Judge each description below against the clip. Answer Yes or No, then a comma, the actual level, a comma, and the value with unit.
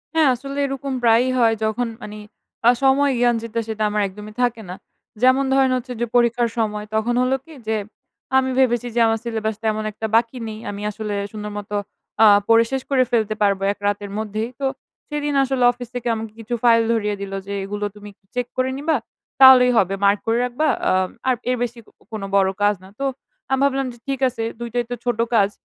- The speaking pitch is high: Yes, high, 235 Hz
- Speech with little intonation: No, average, 3.2 semitones